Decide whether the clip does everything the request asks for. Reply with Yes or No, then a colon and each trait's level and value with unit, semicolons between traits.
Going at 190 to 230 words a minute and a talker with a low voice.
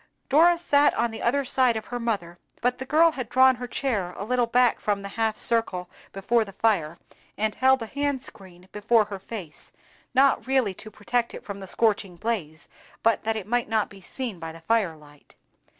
No: fast, 205 wpm; high, 225 Hz